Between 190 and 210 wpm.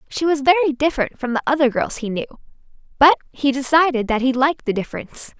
Yes: average, 200 wpm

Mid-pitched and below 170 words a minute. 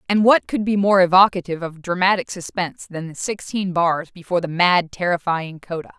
No: medium, 180 Hz; average, 180 wpm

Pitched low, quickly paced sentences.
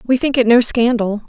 No: high, 235 Hz; fast, 235 wpm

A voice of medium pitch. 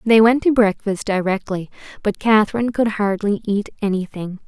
No: high, 210 Hz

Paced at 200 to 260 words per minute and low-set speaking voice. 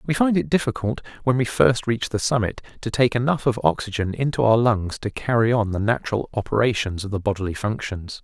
Yes: fast, 205 wpm; low, 115 Hz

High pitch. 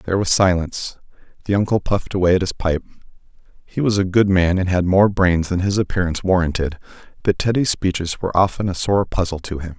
No: very low, 90 Hz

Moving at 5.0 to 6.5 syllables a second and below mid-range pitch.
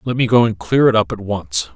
Yes: 5.6 syllables/s; low, 105 Hz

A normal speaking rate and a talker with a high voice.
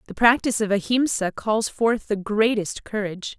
Yes: average, 160 wpm; high, 215 Hz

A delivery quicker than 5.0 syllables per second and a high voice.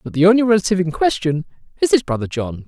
No: 7.2 syllables/s; medium, 180 Hz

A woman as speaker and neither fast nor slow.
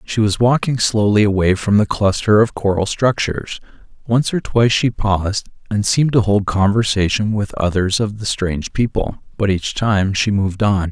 No: male; average, 180 wpm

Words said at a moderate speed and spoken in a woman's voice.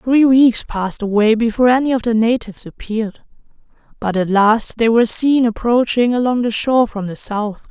Yes: average, 180 wpm; female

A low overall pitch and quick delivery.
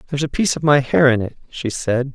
Yes: low, 130 Hz; fast, 280 wpm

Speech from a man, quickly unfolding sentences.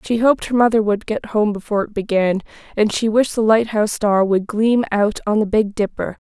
No: female; fast, 220 wpm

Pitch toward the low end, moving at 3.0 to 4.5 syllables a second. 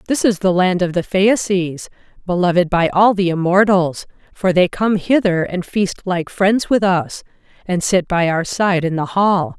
No: medium, 185 Hz; 4.3 syllables/s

